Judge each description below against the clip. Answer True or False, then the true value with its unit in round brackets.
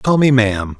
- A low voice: True (120 Hz)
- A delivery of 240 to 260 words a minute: False (230 wpm)